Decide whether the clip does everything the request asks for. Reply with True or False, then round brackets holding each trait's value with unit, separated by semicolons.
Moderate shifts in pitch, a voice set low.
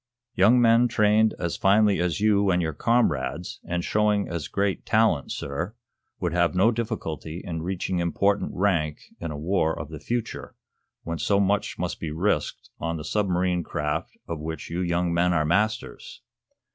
True (4.0 semitones; 90 Hz)